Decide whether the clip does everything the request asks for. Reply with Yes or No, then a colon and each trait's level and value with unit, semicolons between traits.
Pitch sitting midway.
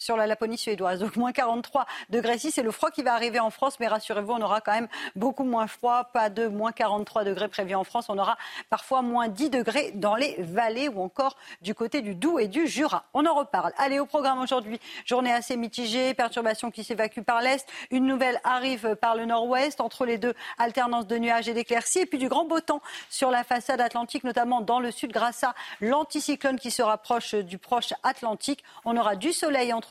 No: high, 240 Hz